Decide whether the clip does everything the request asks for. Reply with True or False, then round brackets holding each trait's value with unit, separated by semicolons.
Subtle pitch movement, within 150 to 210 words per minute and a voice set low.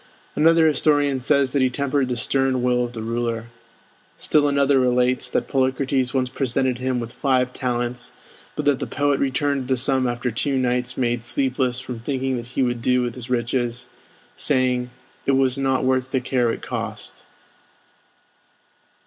True (1.7 semitones; 165 wpm; 130 Hz)